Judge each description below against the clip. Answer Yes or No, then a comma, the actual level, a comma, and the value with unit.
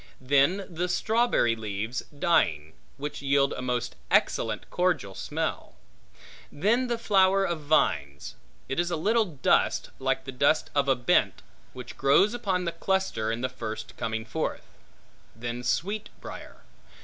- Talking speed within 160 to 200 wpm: No, average, 145 wpm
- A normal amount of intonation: No, wide, 7.6 semitones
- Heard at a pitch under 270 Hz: Yes, medium, 140 Hz